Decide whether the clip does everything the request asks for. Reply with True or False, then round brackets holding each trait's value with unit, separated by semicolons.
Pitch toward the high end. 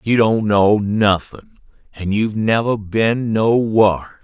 False (105 Hz)